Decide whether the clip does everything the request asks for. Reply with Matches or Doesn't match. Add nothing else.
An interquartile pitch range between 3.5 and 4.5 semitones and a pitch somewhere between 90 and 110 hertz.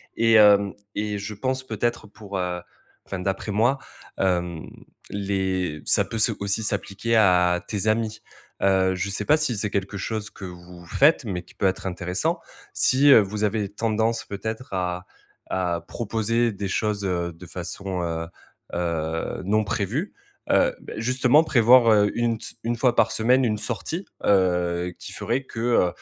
Matches